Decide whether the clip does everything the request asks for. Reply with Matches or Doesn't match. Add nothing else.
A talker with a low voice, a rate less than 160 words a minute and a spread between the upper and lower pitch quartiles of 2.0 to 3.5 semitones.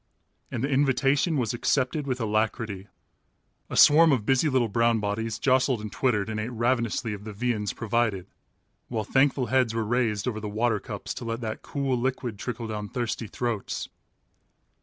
Doesn't match